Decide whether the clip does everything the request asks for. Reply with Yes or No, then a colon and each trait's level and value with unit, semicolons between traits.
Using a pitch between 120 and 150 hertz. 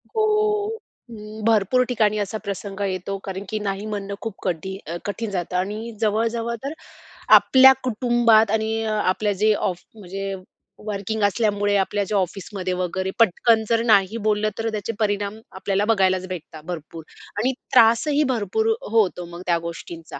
No: high, 210 Hz